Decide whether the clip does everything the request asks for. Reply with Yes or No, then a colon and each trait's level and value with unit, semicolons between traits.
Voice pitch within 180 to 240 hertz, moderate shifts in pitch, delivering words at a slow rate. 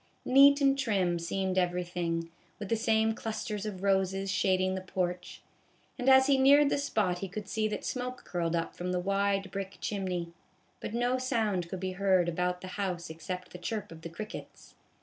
No: high, 190 Hz; average, 3.6 semitones; average, 190 wpm